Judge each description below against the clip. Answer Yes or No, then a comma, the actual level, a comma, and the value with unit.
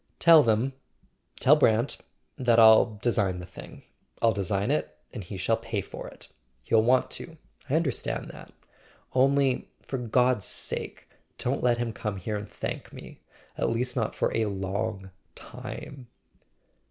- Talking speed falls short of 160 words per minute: Yes, average, 140 wpm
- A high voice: No, low, 115 Hz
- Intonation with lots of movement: No, average, 3.8 semitones